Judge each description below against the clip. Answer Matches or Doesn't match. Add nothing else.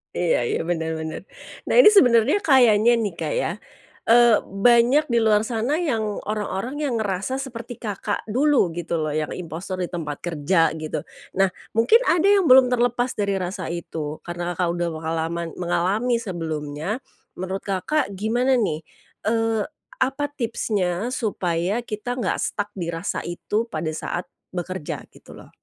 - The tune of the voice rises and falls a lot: Matches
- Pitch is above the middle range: Matches